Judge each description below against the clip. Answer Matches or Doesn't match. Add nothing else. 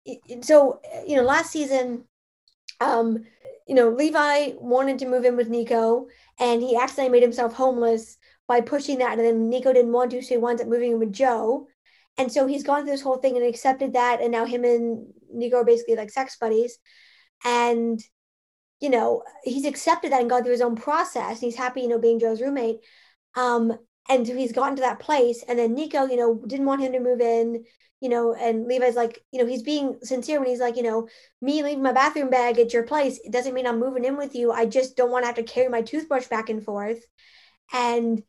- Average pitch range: Doesn't match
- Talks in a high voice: Matches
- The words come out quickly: Matches